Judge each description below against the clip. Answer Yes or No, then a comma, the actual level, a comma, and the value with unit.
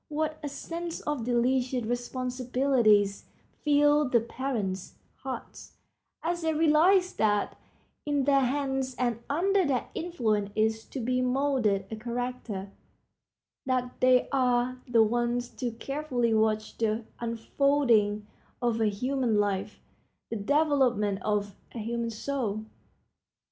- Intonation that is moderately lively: Yes, average, 4.1 semitones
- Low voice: No, very high, 250 Hz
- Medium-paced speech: No, slow, 120 wpm